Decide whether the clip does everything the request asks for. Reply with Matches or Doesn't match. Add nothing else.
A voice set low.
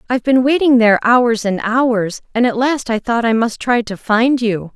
Doesn't match